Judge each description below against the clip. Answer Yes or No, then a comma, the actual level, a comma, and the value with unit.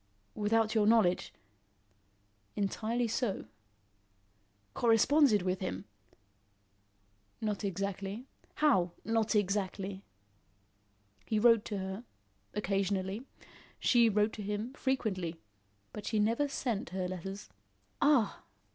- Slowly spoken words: Yes, slow, 95 wpm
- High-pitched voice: Yes, high, 210 Hz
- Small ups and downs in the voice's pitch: No, average, 3.0 semitones